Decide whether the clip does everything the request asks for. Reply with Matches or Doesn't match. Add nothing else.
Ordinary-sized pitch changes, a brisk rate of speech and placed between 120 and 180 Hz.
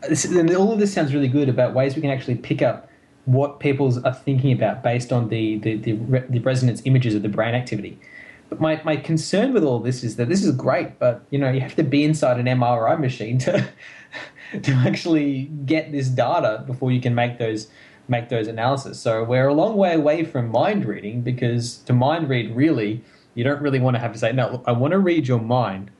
Matches